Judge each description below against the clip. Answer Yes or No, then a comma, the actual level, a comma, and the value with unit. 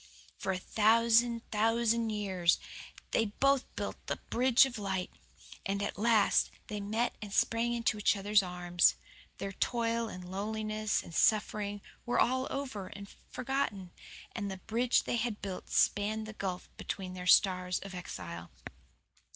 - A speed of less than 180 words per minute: Yes, average, 150 wpm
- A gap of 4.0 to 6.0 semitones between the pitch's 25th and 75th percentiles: No, average, 3.2 semitones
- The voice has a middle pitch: No, high, 210 Hz